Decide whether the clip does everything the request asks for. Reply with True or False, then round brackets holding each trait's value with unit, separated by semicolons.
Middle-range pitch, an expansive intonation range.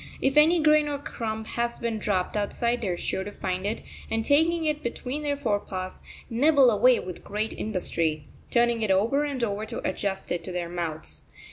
False (225 Hz; 6.3 semitones)